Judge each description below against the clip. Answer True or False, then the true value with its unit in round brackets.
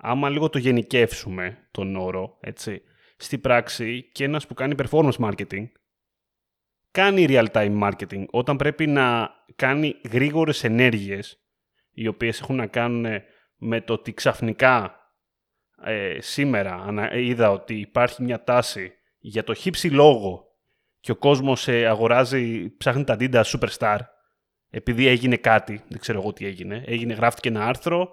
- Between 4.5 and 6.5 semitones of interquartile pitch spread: False (3.5 semitones)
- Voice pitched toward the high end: False (120 Hz)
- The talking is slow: False (140 wpm)